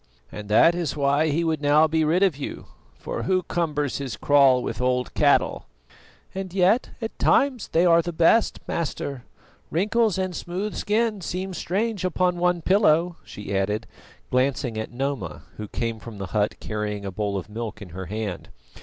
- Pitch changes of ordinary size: No, wide, 8.3 semitones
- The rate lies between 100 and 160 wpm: No, average, 175 wpm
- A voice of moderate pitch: Yes, medium, 150 Hz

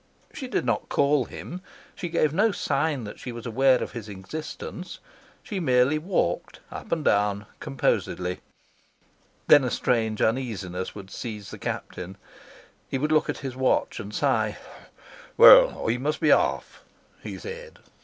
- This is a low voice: Yes, low, 130 Hz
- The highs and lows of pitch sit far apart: Yes, wide, 6.5 semitones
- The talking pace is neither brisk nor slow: Yes, average, 155 wpm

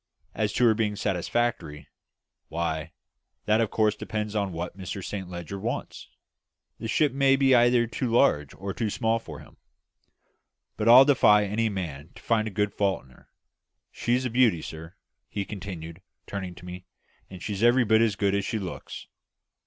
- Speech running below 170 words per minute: No, average, 175 wpm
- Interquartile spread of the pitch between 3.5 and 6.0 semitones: Yes, average, 4.1 semitones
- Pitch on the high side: No, low, 105 Hz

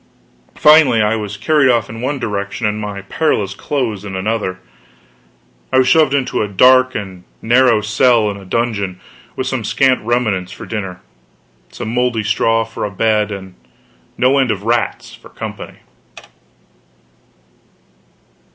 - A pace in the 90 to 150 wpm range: Yes, average, 145 wpm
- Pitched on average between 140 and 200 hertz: No, low, 110 Hz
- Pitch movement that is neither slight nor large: Yes, average, 3.8 semitones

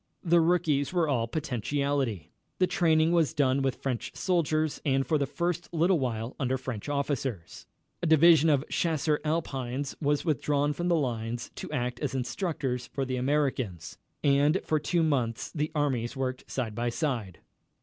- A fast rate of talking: No, average, 160 wpm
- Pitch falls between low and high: Yes, medium, 145 Hz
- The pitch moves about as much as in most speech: Yes, average, 3.8 semitones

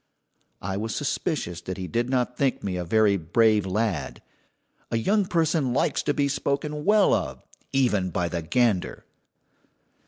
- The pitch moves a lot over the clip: Yes, wide, 7.0 semitones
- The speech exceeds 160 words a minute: No, average, 155 wpm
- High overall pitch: No, low, 115 Hz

